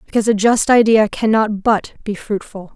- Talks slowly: No, average, 175 wpm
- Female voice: Yes, female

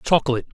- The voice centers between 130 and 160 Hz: Yes, medium, 140 Hz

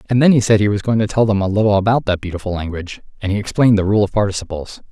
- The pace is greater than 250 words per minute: Yes, fast, 280 wpm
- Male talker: Yes, male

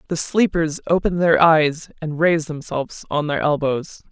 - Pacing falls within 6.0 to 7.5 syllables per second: No, 4.7 syllables/s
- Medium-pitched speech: Yes, medium, 160 Hz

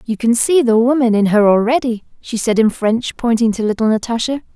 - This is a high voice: Yes, high, 230 Hz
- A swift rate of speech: Yes, fast, 210 wpm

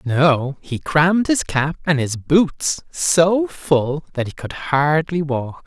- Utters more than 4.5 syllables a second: No, 3.2 syllables/s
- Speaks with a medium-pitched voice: Yes, medium, 155 Hz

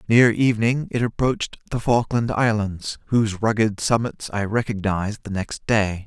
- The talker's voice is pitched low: Yes, low, 110 Hz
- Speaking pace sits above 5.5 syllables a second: No, 4.9 syllables/s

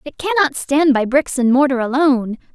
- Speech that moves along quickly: No, average, 190 wpm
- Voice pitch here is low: No, very high, 275 Hz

